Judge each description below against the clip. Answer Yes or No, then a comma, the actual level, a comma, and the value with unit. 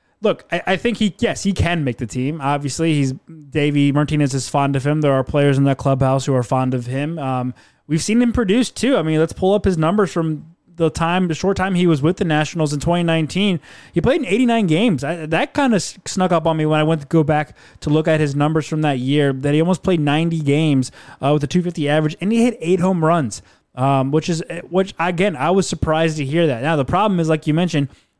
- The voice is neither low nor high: Yes, medium, 160 Hz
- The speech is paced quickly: Yes, fast, 250 wpm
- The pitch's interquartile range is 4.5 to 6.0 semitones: No, average, 3.8 semitones